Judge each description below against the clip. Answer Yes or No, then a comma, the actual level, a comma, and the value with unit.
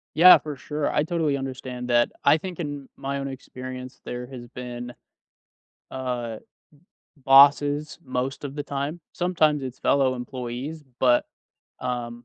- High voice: No, low, 135 Hz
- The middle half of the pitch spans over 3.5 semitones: No, average, 2.9 semitones